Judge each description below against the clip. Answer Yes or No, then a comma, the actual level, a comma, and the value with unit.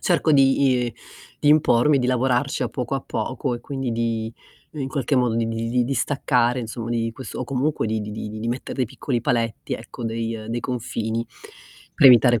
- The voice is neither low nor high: No, low, 120 Hz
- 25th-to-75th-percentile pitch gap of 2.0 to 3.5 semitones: Yes, narrow, 2.5 semitones